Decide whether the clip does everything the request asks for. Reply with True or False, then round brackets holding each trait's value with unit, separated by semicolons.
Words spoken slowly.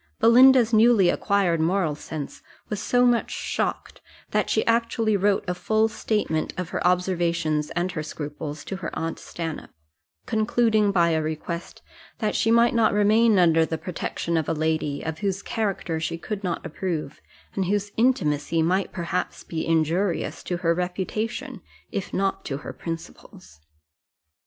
False (155 wpm)